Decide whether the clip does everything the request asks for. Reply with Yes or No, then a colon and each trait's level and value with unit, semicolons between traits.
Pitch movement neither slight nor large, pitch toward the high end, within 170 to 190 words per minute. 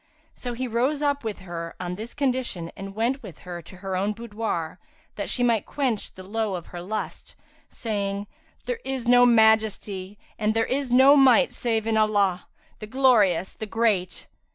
Yes: average, 4.2 semitones; high, 220 Hz; average, 175 wpm